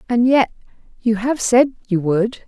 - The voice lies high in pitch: Yes, high, 230 Hz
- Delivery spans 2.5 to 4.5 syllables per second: Yes, 4.1 syllables/s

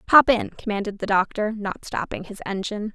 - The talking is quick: No, average, 185 wpm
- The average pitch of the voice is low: No, high, 210 Hz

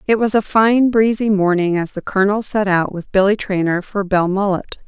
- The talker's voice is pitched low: No, high, 200 Hz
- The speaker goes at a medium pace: Yes, average, 195 wpm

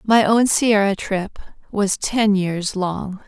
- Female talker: Yes, female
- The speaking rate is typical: Yes, average, 145 wpm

